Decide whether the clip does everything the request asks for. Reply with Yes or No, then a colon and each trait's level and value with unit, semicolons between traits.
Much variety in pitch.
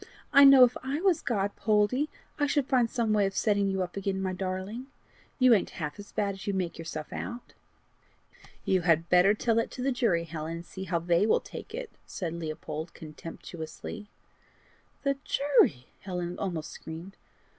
Yes: wide, 5.8 semitones